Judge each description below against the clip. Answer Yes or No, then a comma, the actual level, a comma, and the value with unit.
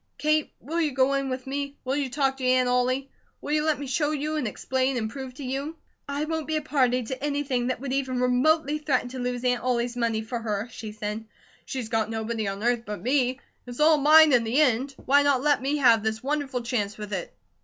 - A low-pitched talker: No, very high, 255 Hz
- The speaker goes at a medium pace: No, fast, 235 wpm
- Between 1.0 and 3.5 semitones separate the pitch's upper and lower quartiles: Yes, average, 3.1 semitones